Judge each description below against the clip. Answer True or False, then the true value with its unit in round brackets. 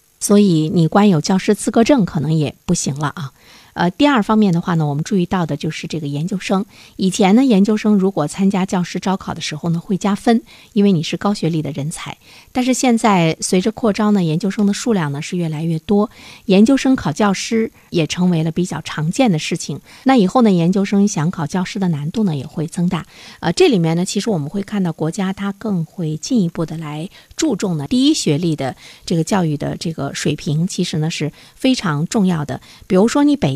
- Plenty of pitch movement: False (4.4 semitones)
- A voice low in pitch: False (185 Hz)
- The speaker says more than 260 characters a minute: True (320 characters per minute)